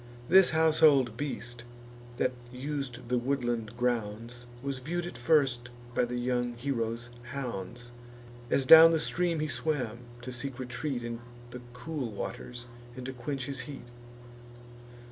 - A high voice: No, low, 125 Hz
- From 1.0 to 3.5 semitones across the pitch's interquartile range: Yes, average, 2.8 semitones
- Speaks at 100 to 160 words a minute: Yes, average, 140 wpm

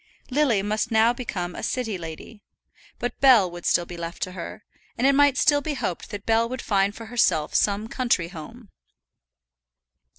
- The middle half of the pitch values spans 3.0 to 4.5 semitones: No, average, 5.2 semitones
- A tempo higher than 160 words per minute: Yes, average, 175 wpm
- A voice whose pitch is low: No, high, 220 Hz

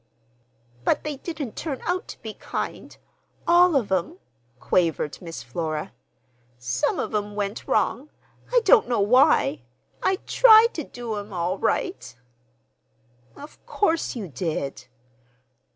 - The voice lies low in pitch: No, high, 215 Hz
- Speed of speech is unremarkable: No, slow, 125 wpm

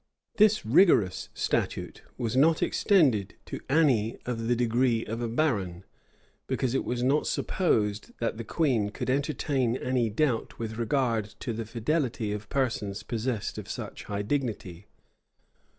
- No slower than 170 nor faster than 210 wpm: No, average, 145 wpm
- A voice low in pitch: Yes, low, 120 Hz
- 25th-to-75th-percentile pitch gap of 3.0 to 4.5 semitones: Yes, average, 3.8 semitones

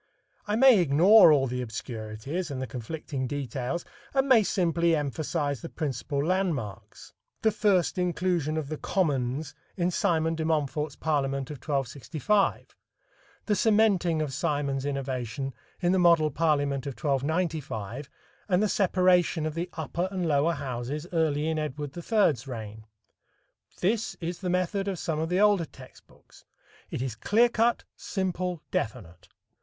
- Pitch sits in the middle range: Yes, medium, 155 Hz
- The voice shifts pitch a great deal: No, average, 4.7 semitones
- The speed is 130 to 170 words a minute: Yes, average, 145 wpm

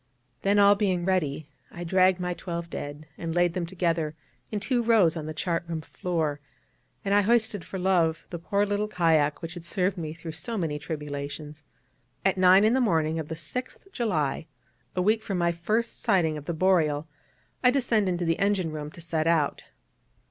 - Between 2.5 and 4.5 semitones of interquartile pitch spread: Yes, average, 3.8 semitones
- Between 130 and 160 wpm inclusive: No, average, 190 wpm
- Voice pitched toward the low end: No, medium, 175 Hz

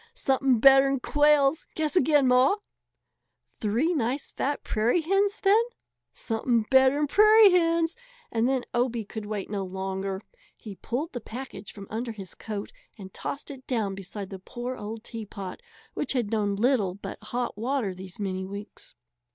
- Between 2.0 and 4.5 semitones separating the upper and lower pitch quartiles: No, average, 5.3 semitones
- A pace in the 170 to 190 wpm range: No, average, 155 wpm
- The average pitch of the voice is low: No, high, 240 Hz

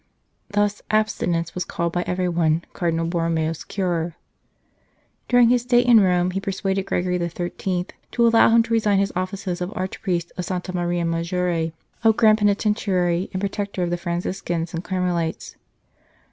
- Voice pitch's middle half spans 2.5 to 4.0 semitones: Yes, average, 2.8 semitones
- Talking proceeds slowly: No, average, 160 wpm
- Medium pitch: Yes, medium, 180 Hz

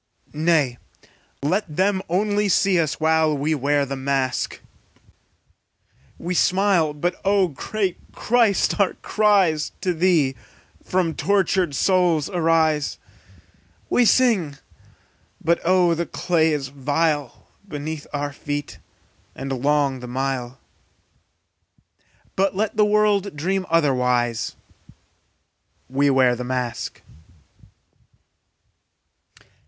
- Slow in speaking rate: Yes, slow, 100 wpm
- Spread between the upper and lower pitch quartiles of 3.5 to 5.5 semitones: Yes, average, 5.1 semitones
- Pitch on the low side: No, medium, 160 Hz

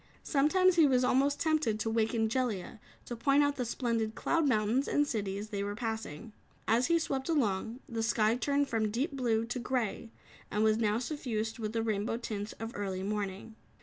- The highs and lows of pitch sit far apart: No, average, 3.7 semitones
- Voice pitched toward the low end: No, high, 230 Hz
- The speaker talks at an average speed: Yes, average, 185 wpm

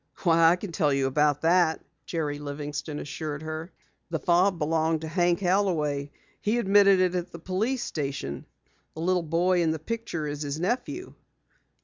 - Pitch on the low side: No, medium, 165 Hz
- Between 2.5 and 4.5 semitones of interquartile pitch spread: Yes, average, 3.5 semitones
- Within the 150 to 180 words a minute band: Yes, average, 165 wpm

